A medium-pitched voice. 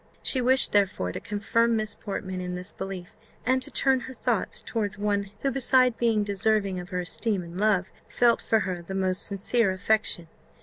No: high, 205 Hz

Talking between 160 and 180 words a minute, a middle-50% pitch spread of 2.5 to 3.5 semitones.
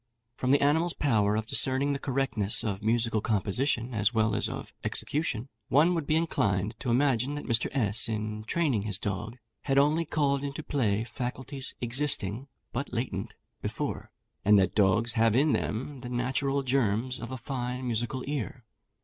No: average, 165 wpm; average, 4.1 semitones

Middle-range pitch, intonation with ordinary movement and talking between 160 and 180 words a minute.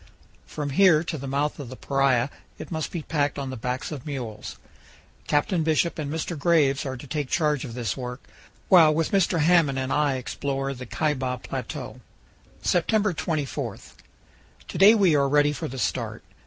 Yes: medium, 145 Hz; average, 3.2 semitones; average, 175 wpm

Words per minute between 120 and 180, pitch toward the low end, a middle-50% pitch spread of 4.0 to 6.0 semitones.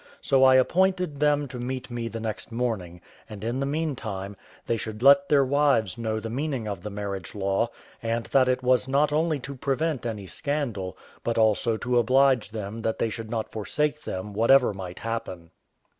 No: average, 190 wpm; low, 120 Hz; average, 4.3 semitones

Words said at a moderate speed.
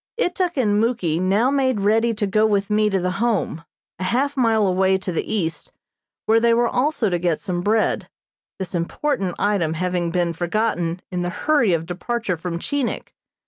Yes: average, 185 wpm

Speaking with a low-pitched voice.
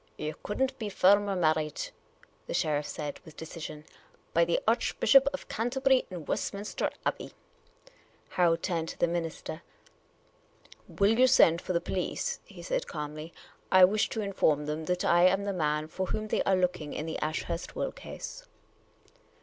No: medium, 180 Hz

